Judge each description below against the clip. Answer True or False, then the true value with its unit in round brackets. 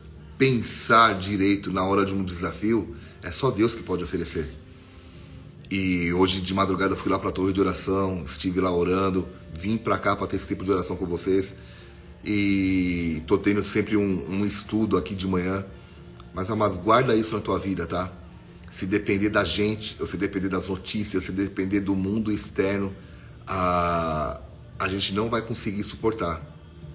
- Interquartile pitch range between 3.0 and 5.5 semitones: False (2.4 semitones)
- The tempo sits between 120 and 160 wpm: False (175 wpm)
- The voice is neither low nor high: False (95 Hz)